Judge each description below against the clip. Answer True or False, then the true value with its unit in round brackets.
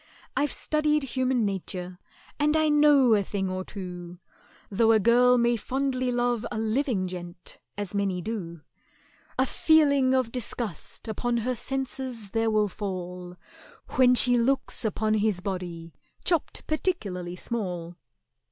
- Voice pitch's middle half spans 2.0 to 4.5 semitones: False (5.6 semitones)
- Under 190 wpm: True (135 wpm)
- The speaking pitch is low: False (225 Hz)